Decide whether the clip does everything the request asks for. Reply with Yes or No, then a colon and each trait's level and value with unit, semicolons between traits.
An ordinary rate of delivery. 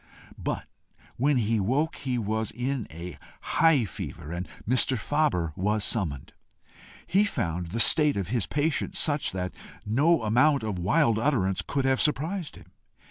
Yes: average, 150 wpm